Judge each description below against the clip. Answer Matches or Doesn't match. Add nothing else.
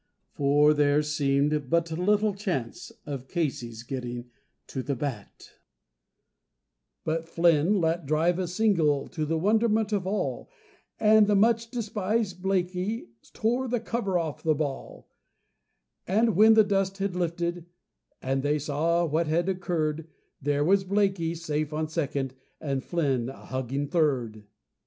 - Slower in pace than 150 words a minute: Matches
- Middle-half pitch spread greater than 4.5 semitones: Matches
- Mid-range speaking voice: Matches